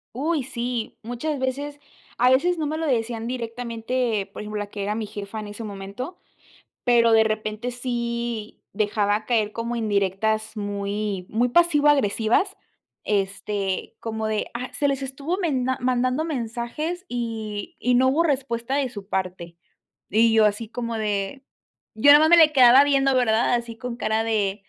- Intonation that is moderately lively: Yes, average, 3.6 semitones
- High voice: Yes, high, 235 Hz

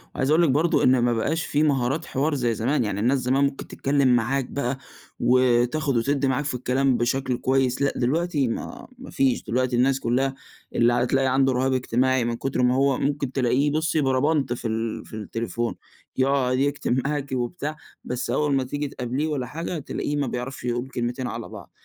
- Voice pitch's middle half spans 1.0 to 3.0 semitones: Yes, narrow, 2.4 semitones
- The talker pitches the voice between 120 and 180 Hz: Yes, low, 130 Hz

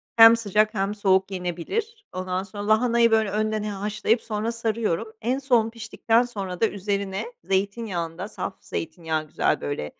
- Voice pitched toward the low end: No, high, 210 Hz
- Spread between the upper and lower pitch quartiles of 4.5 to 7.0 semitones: No, average, 3.2 semitones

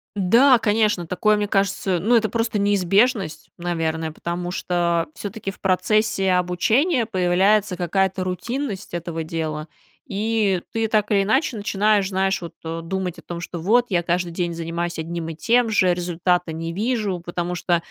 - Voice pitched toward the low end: No, medium, 185 Hz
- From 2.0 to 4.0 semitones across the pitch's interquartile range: Yes, average, 3.5 semitones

